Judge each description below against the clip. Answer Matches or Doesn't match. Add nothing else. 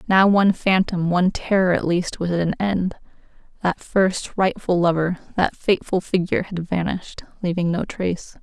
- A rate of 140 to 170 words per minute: Matches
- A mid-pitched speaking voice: Matches